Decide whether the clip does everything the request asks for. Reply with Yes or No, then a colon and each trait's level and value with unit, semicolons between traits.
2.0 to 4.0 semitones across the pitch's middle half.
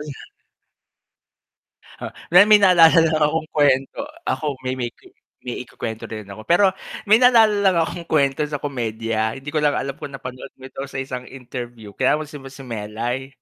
No: average, 4.7 semitones